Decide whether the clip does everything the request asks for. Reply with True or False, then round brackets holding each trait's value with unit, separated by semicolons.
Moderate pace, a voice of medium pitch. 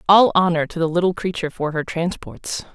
True (195 wpm; 175 Hz)